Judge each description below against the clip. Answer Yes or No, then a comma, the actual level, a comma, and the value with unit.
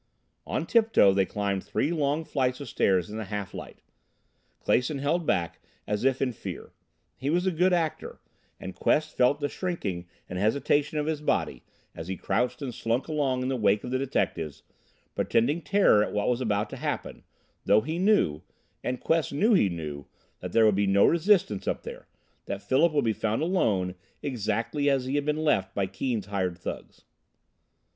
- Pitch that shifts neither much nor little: No, wide, 6.9 semitones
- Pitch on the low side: Yes, low, 125 Hz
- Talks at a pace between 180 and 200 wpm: Yes, average, 185 wpm